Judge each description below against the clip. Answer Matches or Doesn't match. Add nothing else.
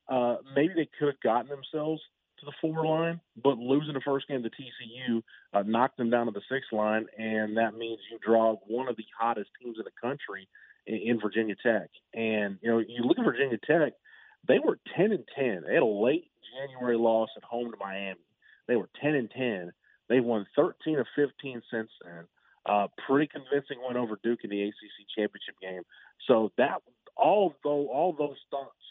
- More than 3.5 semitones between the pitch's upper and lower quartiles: Matches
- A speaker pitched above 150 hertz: Doesn't match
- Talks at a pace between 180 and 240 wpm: Matches